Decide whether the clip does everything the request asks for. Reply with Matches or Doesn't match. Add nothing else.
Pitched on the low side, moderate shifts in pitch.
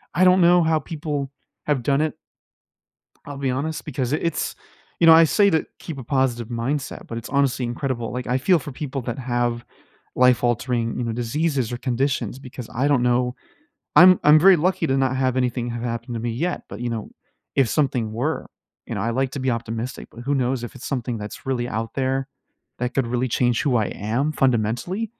Matches